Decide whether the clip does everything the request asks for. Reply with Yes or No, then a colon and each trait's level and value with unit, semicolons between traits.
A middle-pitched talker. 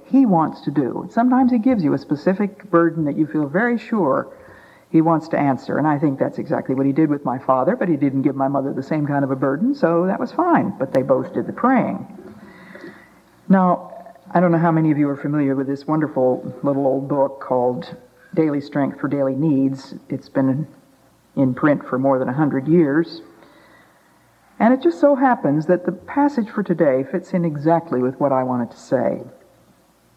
Yes: medium, 155 Hz